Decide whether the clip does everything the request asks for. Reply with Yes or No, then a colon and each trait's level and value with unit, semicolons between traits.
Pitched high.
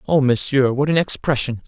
No: low, 135 Hz